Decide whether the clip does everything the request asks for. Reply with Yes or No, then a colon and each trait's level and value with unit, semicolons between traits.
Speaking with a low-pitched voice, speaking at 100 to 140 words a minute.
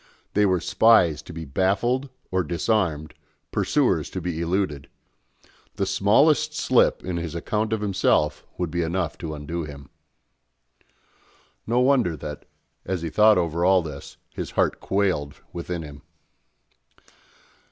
Yes: very low, 90 Hz; slow, 135 wpm